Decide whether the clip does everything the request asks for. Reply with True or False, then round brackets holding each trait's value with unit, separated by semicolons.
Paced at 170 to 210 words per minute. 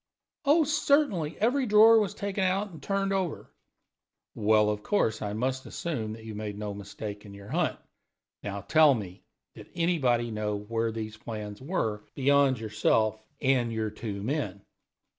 False (155 wpm)